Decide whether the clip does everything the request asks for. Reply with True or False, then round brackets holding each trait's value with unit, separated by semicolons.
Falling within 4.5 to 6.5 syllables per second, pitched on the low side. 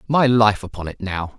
True (5.0 syllables/s; 110 Hz)